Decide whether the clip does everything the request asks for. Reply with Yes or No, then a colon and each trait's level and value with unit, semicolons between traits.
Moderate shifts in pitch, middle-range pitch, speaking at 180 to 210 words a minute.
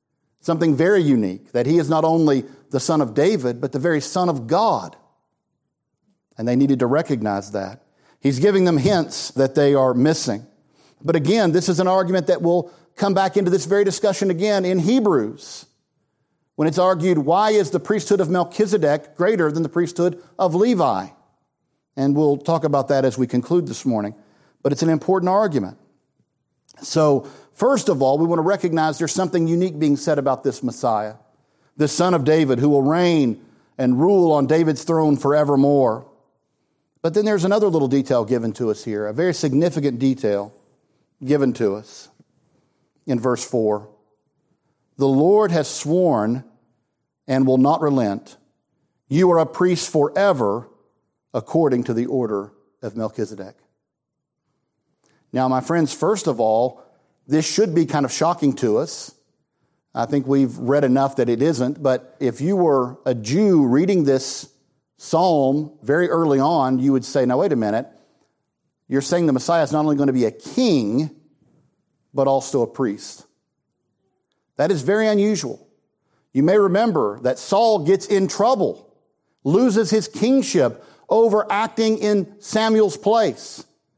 No: average, 5.0 semitones; medium, 150 Hz; average, 160 wpm